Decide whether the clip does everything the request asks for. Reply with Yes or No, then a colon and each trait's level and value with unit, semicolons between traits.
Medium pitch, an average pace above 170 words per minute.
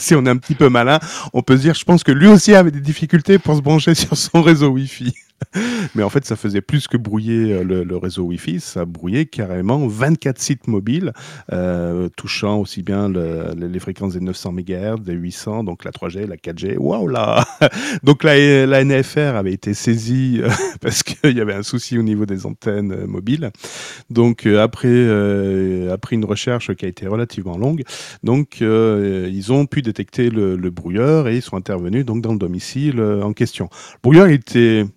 No: low, 115 Hz; average, 195 wpm